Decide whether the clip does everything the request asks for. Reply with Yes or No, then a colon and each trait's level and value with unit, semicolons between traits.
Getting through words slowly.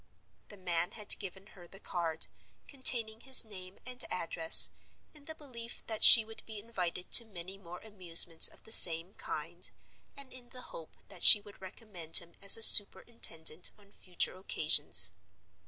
No: average, 165 wpm